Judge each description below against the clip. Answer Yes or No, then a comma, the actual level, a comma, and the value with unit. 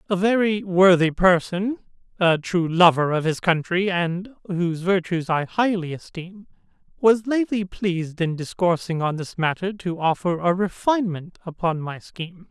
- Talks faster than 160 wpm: No, average, 150 wpm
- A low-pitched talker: No, medium, 180 Hz